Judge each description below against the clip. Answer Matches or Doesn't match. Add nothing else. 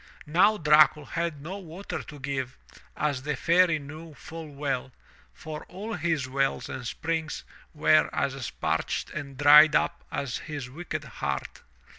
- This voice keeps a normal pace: Matches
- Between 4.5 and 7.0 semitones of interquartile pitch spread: Doesn't match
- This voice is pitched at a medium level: Matches